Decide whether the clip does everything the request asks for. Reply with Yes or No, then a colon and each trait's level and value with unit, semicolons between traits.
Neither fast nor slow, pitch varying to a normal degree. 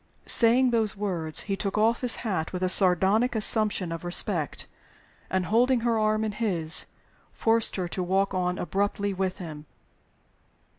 Yes: average, 155 wpm; average, 3.5 semitones